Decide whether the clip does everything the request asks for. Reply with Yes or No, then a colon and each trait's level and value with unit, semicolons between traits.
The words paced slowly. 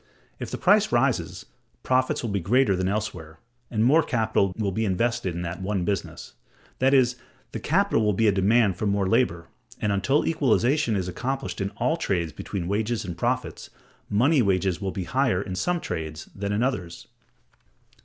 No: average, 180 wpm